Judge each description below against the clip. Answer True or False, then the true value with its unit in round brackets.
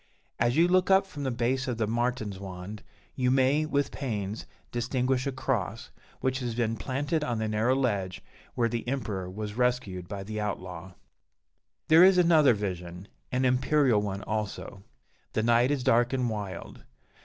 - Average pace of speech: True (165 wpm)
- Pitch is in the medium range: False (120 Hz)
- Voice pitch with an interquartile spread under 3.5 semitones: False (4.1 semitones)